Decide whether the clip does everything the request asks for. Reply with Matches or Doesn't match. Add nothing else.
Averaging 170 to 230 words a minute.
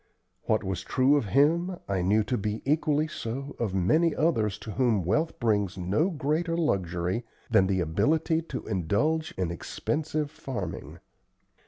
Doesn't match